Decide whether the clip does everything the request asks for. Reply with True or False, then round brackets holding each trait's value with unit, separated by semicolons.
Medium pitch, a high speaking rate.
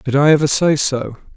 True (145 Hz; 220 wpm)